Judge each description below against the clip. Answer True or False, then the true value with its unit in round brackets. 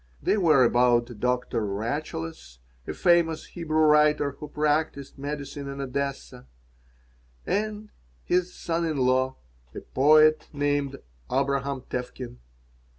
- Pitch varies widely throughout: False (3.5 semitones)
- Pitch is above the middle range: False (140 Hz)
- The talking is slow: True (110 wpm)